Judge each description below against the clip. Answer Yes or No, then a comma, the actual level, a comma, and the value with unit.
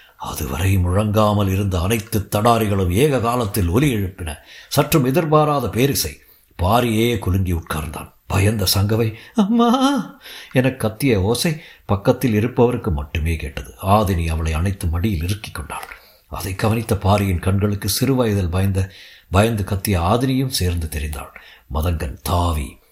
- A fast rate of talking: No, average, 115 wpm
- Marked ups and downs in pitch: No, average, 4.9 semitones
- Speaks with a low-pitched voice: Yes, low, 100 Hz